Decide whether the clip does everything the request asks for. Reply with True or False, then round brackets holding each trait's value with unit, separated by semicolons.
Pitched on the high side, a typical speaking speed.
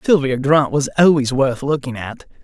False (140 Hz; 175 wpm)